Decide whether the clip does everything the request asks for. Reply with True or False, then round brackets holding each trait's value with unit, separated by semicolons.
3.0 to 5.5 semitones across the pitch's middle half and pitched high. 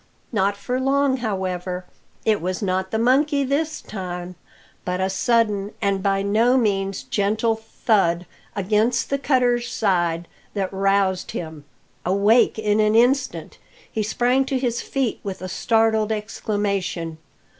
True (4.0 semitones; 210 Hz)